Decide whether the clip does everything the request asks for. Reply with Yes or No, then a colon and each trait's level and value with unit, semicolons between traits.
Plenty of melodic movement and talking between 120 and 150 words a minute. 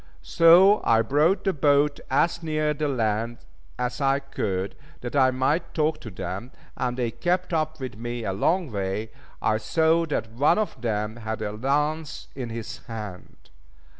No: wide, 5.8 semitones; average, 165 wpm